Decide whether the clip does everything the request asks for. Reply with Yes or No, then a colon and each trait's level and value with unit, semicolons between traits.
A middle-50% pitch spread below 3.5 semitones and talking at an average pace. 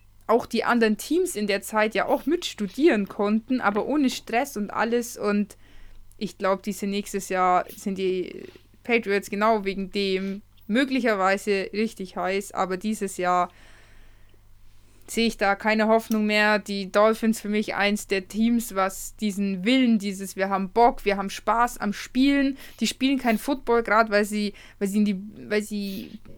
Yes: narrow, 2.6 semitones; average, 165 wpm